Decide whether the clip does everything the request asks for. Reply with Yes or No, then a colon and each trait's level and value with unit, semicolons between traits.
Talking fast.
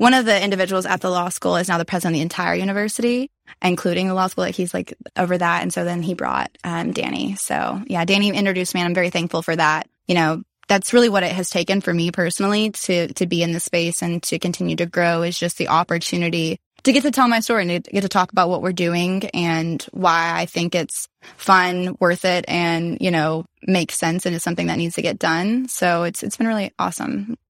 Yes: fast, 245 wpm